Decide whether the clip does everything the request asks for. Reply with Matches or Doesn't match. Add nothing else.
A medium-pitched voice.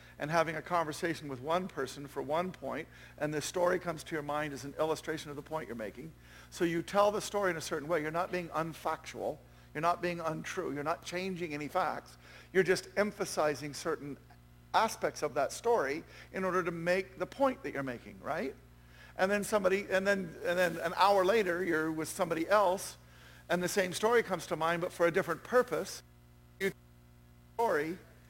Matches